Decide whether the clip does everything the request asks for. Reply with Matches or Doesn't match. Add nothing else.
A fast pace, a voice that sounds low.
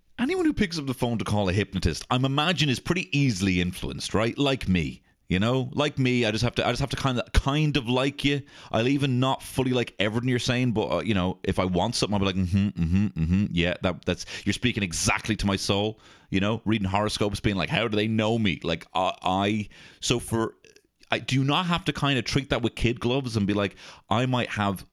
Matches